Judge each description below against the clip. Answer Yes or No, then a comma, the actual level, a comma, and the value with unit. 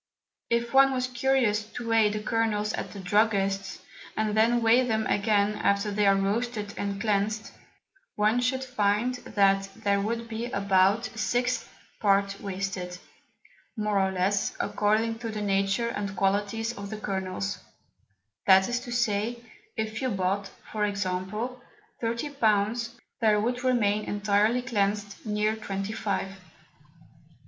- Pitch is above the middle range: Yes, high, 210 Hz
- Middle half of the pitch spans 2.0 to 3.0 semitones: Yes, narrow, 2.6 semitones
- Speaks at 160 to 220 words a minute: No, average, 140 wpm